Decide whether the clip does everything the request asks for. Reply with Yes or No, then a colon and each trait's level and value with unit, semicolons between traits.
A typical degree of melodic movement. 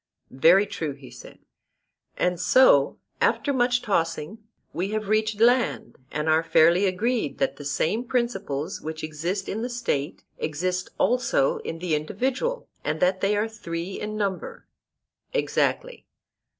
No: wide, 6.1 semitones